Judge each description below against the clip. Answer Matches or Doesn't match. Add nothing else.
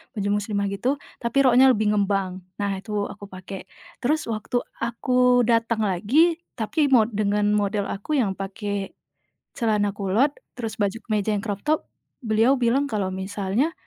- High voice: Matches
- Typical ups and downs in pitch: Matches